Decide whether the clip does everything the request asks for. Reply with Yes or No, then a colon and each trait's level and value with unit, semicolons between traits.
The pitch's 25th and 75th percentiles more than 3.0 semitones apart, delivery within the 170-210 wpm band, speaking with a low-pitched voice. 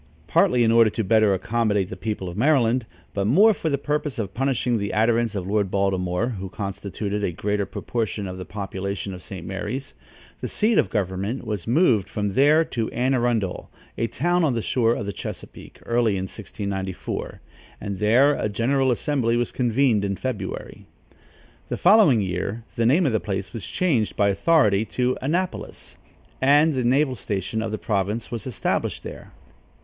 Yes: average, 4.4 semitones; average, 175 wpm; low, 110 Hz